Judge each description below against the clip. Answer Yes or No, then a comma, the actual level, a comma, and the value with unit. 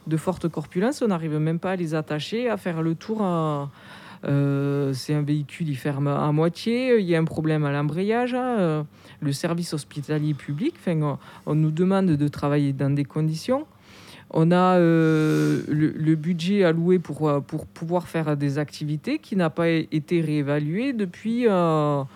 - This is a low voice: No, medium, 160 Hz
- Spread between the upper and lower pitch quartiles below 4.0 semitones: Yes, average, 3.4 semitones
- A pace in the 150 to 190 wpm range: Yes, average, 180 wpm